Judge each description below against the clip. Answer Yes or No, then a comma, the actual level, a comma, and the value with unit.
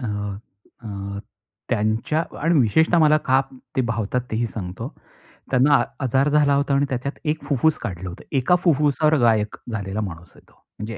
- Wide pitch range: Yes, wide, 5.8 semitones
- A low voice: Yes, low, 125 Hz